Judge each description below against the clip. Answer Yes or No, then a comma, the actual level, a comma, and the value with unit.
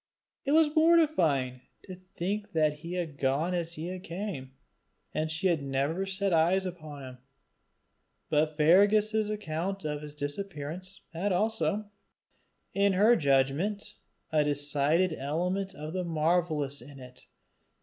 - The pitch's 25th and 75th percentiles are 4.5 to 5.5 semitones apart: Yes, average, 4.9 semitones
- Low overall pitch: No, medium, 170 Hz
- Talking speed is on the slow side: Yes, slow, 130 wpm